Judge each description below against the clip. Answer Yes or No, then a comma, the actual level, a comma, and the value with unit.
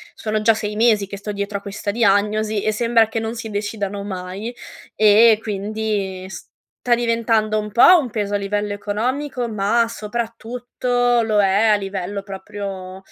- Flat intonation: Yes, narrow, 2.2 semitones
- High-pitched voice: Yes, high, 215 Hz